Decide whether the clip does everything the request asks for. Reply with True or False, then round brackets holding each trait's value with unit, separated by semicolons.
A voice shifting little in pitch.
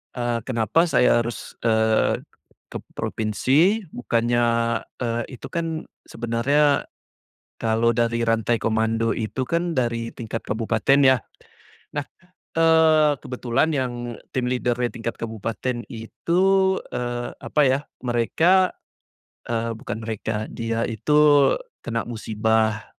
False (3.1 semitones)